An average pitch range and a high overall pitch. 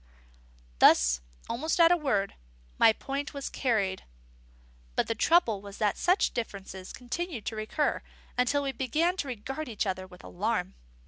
No: wide, 6.3 semitones; high, 240 Hz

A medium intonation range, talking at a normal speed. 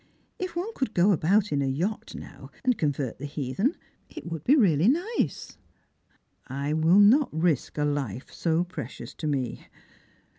No: wide, 7.2 semitones; average, 165 wpm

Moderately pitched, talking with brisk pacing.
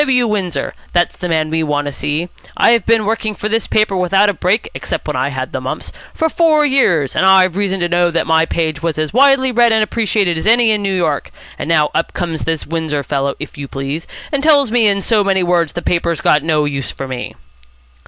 Yes: medium, 180 Hz; fast, 230 wpm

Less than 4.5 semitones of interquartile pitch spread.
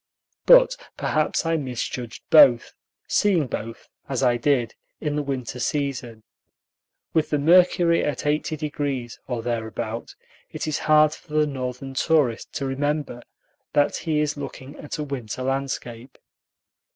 Yes: average, 3.6 semitones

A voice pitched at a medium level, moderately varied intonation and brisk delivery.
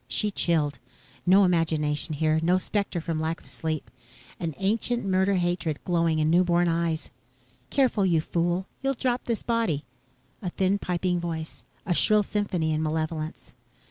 No: medium, 175 Hz; average, 3.3 semitones; average, 150 wpm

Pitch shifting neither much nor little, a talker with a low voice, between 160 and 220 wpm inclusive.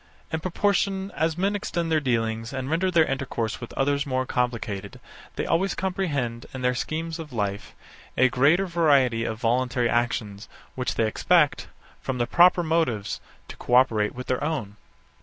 No: wide, 5.8 semitones; low, 130 Hz; average, 165 wpm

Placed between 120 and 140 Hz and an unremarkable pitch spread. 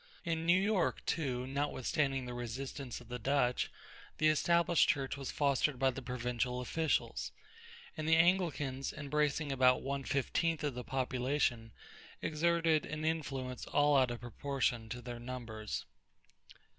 Yes: low, 135 Hz; average, 3.6 semitones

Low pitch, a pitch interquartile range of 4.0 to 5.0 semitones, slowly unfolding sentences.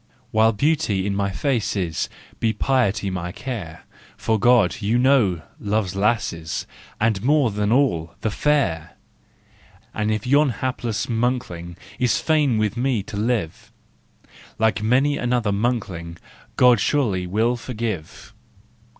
Yes: low, 110 Hz; average, 4.3 semitones; slow, 130 wpm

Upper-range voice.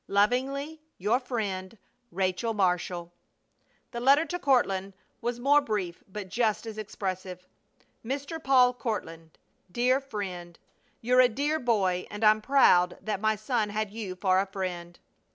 Yes: high, 215 Hz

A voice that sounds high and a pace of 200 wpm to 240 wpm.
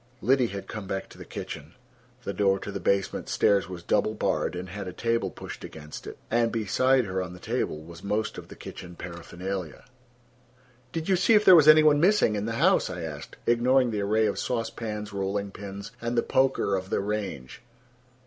No: low, 105 Hz; fast, 205 wpm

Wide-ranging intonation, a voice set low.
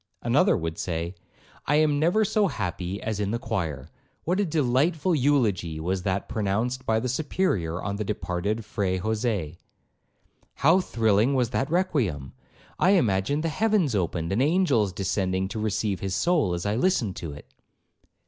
Yes: wide, 7.8 semitones; low, 110 Hz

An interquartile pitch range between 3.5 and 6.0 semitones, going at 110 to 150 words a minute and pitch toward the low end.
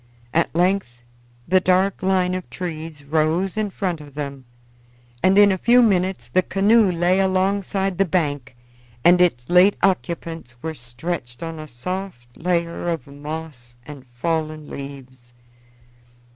No: average, 4.6 semitones; average, 140 wpm; medium, 170 Hz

